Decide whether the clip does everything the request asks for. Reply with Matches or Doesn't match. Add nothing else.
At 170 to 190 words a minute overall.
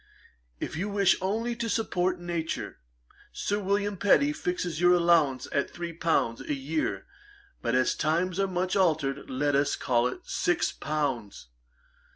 Doesn't match